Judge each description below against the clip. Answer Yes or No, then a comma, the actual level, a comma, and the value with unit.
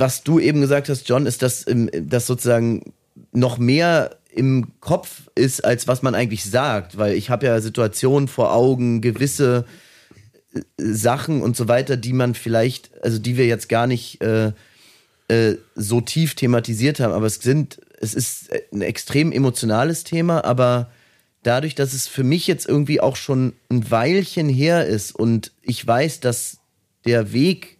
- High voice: No, low, 125 Hz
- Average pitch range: Yes, average, 3.3 semitones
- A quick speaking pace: No, average, 165 wpm